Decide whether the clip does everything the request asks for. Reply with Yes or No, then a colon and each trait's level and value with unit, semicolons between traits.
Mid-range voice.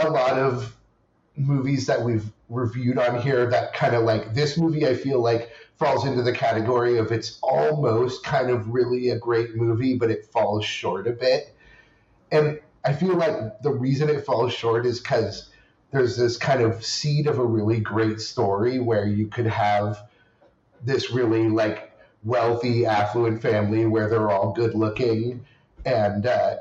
No: low, 120 Hz